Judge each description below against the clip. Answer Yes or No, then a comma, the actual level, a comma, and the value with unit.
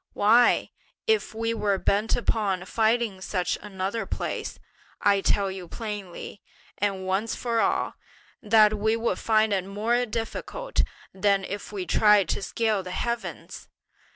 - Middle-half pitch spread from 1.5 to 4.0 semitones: Yes, average, 2.7 semitones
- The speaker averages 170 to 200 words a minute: No, average, 140 wpm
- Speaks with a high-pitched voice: Yes, high, 210 Hz